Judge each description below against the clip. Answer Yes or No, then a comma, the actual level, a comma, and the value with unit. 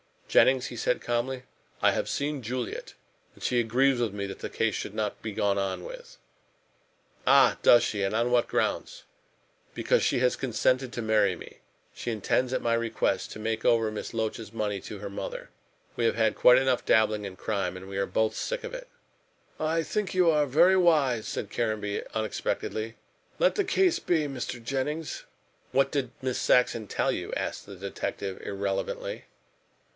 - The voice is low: Yes, low, 120 Hz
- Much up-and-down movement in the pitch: No, average, 4.0 semitones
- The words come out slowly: No, average, 180 wpm